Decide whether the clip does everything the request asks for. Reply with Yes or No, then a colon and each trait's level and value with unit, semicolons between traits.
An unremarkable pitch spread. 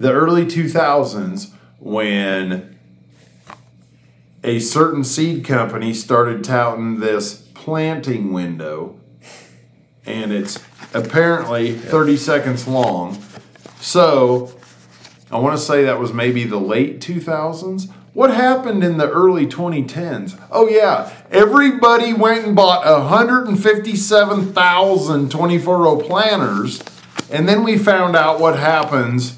No: wide, 8.0 semitones